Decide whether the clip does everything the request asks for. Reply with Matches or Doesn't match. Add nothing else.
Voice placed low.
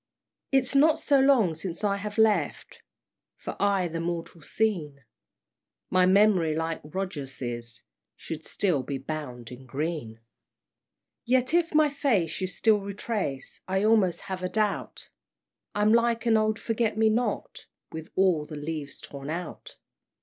Doesn't match